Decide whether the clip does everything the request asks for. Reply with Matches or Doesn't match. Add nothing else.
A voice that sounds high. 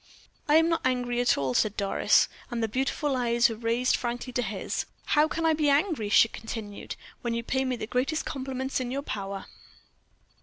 Matches